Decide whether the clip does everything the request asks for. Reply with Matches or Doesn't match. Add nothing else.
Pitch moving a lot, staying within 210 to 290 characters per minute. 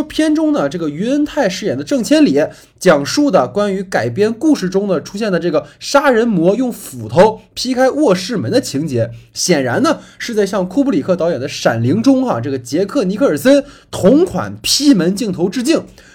Matches